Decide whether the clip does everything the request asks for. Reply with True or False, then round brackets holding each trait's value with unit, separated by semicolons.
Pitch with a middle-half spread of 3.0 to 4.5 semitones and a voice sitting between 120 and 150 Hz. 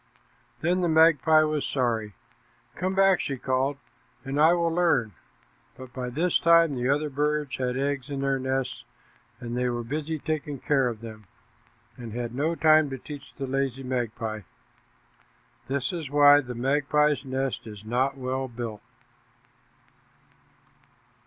True (3.4 semitones; 135 Hz)